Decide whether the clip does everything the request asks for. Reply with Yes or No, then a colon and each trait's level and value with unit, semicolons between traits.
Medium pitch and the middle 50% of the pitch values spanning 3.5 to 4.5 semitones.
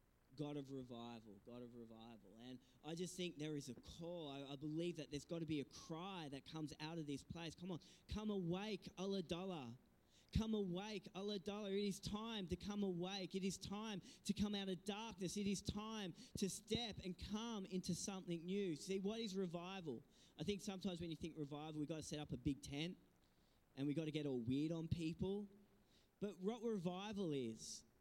No: medium, 175 Hz; average, 5.0 semitones